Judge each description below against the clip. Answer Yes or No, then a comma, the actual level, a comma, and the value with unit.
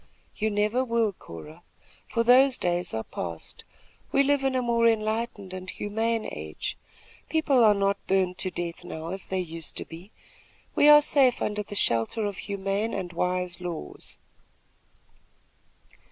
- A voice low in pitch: No, high, 200 Hz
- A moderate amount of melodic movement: Yes, average, 4.6 semitones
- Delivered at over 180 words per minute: No, average, 155 wpm